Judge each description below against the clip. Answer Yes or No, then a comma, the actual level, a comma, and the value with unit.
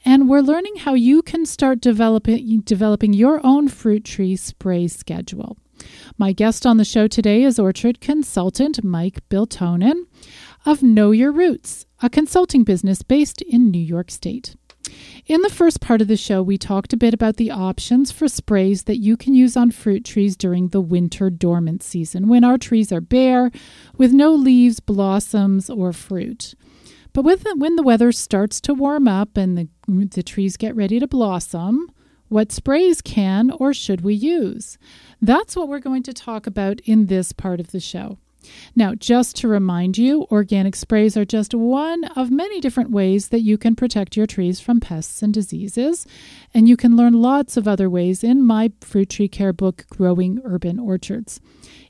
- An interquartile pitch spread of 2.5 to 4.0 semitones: No, average, 4.7 semitones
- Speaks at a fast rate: No, average, 180 wpm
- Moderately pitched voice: No, high, 225 Hz